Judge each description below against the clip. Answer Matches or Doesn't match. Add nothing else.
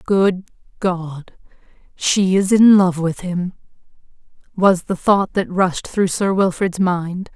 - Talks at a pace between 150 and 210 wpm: Doesn't match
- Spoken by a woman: Matches